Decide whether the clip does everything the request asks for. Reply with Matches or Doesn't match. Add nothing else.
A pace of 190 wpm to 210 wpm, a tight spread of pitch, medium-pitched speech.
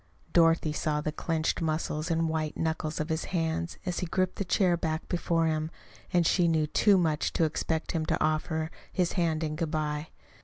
Matches